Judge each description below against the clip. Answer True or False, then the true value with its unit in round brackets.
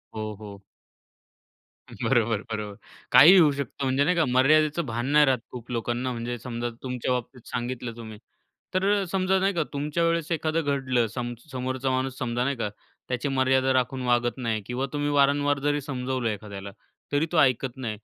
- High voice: False (130 Hz)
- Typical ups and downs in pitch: True (3.2 semitones)